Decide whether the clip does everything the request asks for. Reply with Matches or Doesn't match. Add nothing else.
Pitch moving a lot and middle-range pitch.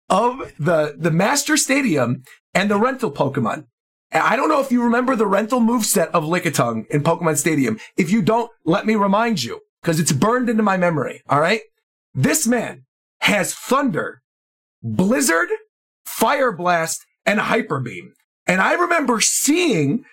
Doesn't match